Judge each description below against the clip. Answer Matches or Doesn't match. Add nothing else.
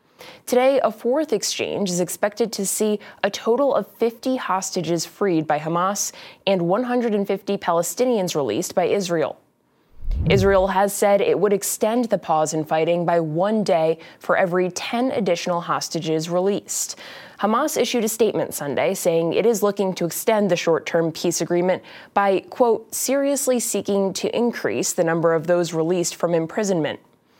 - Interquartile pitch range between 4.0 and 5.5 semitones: Matches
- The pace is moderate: Matches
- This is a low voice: Doesn't match